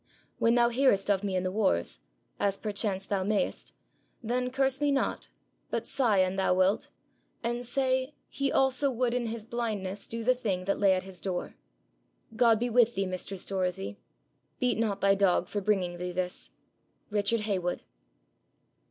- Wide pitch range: No, average, 4.2 semitones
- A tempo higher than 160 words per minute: Yes, average, 170 wpm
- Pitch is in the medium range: No, high, 205 Hz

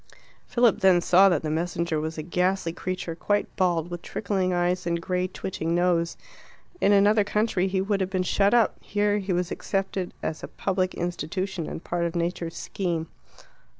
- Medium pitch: Yes, medium, 180 Hz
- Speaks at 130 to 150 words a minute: No, average, 180 wpm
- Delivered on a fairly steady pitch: Yes, narrow, 2.3 semitones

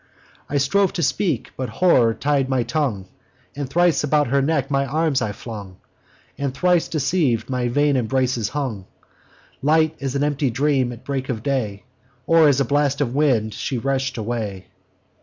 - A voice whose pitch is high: No, low, 135 Hz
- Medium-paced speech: Yes, average, 170 wpm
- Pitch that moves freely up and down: No, average, 3.4 semitones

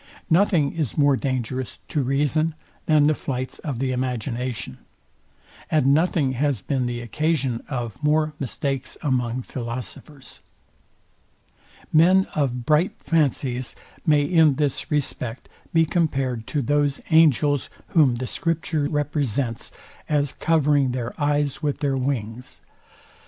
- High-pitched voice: No, medium, 140 Hz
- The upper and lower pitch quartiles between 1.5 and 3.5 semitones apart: Yes, average, 3.2 semitones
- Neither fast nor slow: No, slow, 120 wpm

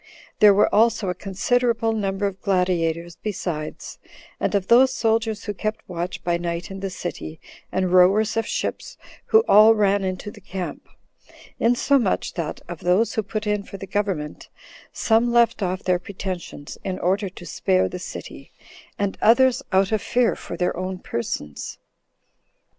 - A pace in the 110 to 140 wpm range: No, average, 160 wpm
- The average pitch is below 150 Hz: No, high, 195 Hz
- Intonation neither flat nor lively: Yes, average, 3.5 semitones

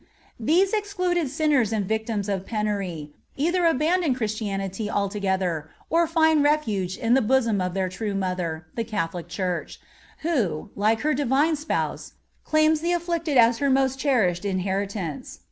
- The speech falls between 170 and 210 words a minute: No, average, 145 wpm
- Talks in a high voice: Yes, high, 225 Hz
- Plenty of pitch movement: Yes, wide, 7.9 semitones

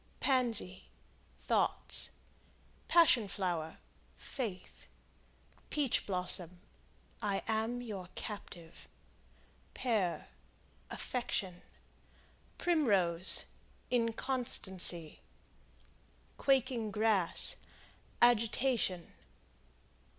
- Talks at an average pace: No, slow, 55 wpm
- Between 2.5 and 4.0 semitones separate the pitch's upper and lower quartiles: No, average, 5.1 semitones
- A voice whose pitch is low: No, high, 215 Hz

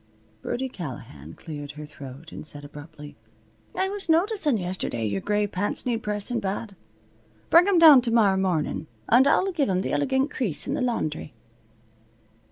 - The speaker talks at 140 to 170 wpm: Yes, average, 160 wpm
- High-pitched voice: Yes, high, 200 Hz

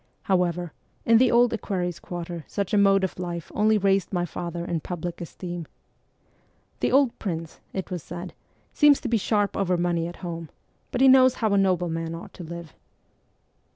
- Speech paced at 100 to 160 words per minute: No, average, 190 wpm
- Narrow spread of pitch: No, average, 3.2 semitones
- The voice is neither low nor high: Yes, medium, 180 Hz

